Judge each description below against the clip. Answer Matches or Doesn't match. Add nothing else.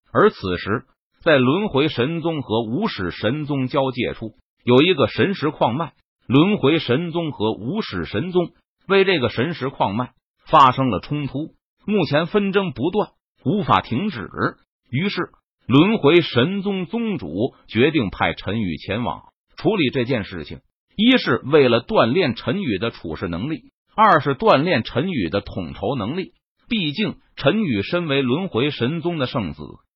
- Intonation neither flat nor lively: Doesn't match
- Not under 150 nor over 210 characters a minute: Doesn't match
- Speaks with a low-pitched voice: Doesn't match